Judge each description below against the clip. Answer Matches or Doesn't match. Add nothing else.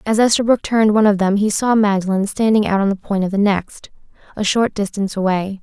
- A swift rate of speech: Matches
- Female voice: Matches